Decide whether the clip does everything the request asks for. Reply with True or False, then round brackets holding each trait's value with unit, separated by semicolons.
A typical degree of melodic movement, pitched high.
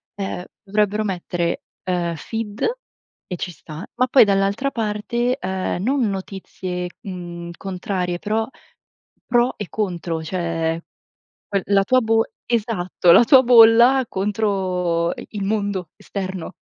True (3.7 semitones; 195 Hz)